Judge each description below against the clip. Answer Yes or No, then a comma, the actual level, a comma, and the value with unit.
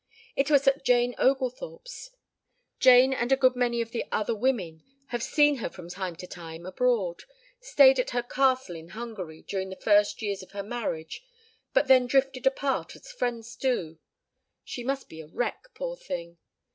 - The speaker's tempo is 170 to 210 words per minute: Yes, average, 175 wpm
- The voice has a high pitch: Yes, high, 240 Hz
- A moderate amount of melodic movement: No, wide, 6.0 semitones